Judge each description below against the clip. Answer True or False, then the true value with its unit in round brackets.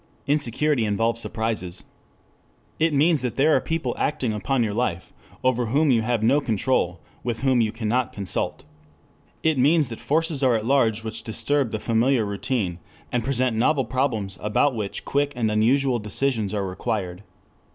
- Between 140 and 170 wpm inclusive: True (160 wpm)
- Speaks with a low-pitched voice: True (120 Hz)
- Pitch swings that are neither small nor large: True (4.1 semitones)